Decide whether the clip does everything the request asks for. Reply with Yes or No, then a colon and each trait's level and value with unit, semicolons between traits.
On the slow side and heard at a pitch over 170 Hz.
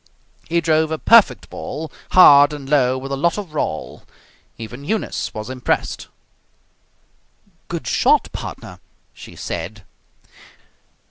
No: slow, 120 wpm; medium, 145 Hz